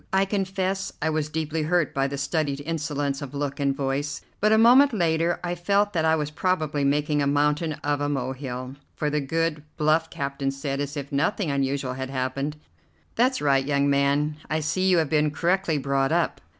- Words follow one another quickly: No, average, 195 wpm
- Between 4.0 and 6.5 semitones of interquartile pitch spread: No, average, 2.9 semitones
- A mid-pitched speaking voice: Yes, medium, 150 Hz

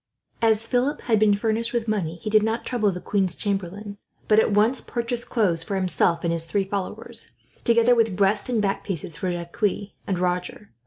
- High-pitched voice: Yes, high, 205 Hz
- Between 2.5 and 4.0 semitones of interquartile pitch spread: Yes, average, 3.6 semitones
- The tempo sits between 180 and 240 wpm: Yes, average, 195 wpm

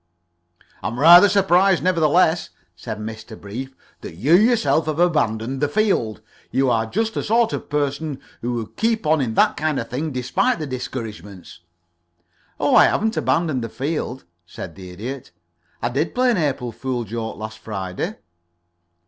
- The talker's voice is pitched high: No, low, 135 Hz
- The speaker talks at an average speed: Yes, average, 165 wpm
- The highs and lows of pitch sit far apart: Yes, wide, 7.4 semitones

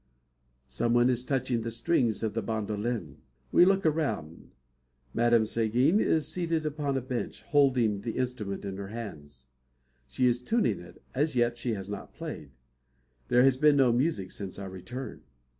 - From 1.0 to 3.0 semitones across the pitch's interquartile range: No, average, 4.4 semitones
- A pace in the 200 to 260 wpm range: No, average, 160 wpm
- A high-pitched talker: No, low, 120 Hz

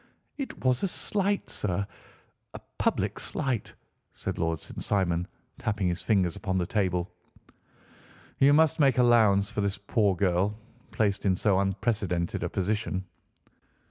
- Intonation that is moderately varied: Yes, average, 3.9 semitones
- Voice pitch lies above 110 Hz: No, low, 100 Hz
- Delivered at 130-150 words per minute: Yes, average, 140 wpm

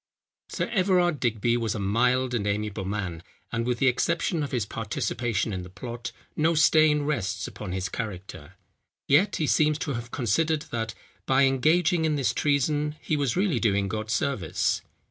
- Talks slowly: No, average, 170 wpm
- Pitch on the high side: No, low, 125 Hz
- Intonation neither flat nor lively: No, wide, 5.9 semitones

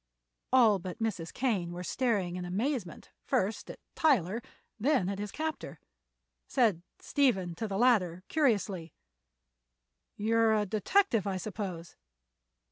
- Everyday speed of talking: No, slow, 125 wpm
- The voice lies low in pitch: No, high, 210 Hz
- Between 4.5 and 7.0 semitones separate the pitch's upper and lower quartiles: Yes, average, 5.0 semitones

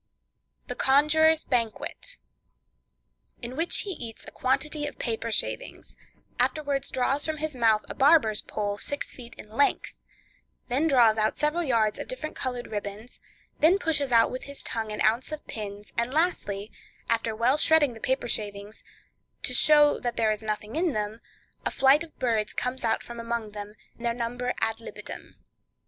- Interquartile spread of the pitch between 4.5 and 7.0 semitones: Yes, average, 5.1 semitones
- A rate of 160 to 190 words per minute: Yes, average, 165 wpm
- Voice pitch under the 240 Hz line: No, high, 245 Hz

